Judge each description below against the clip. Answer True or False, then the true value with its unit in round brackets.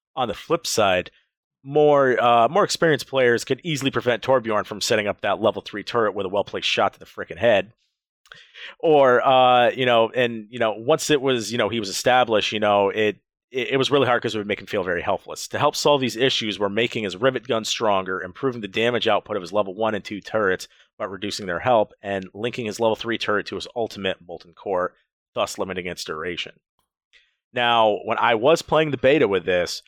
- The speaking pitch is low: True (120 Hz)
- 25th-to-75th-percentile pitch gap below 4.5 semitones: True (3.9 semitones)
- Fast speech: True (220 wpm)